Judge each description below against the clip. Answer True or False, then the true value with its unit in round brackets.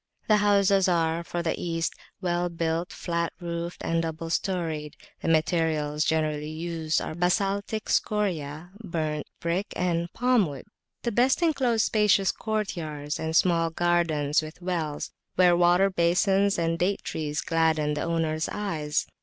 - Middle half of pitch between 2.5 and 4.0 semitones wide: True (3.2 semitones)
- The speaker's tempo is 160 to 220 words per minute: False (145 wpm)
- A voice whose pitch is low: False (170 Hz)